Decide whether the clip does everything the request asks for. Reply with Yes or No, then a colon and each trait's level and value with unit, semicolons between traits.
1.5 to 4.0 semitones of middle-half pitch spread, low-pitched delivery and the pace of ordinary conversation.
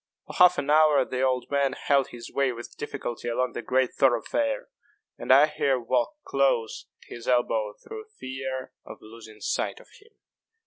Yes: average, 2.9 semitones; low, 130 Hz; average, 175 wpm